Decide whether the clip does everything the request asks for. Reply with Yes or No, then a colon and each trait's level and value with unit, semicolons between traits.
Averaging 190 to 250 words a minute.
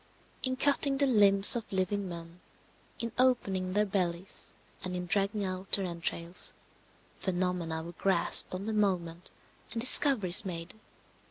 No: average, 140 wpm